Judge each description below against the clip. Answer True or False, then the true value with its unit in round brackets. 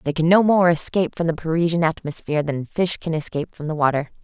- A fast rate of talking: True (225 wpm)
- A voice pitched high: False (160 Hz)